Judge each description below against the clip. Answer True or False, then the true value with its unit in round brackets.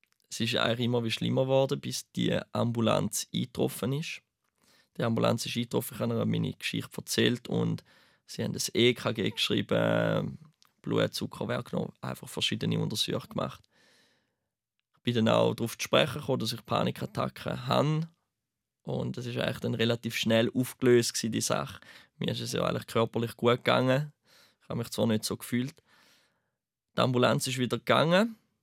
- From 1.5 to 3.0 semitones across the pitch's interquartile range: True (2.5 semitones)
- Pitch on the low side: True (120 Hz)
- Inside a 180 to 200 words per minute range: False (155 wpm)